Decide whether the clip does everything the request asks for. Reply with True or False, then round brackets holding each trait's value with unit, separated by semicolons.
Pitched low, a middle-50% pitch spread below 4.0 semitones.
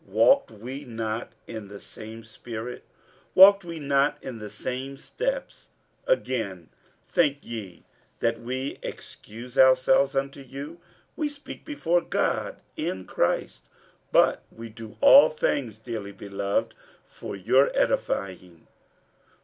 False (125 Hz; 4.5 semitones)